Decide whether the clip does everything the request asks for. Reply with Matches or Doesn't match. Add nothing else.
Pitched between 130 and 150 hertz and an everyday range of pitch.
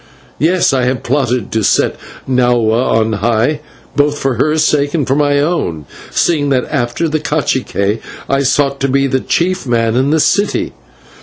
Matches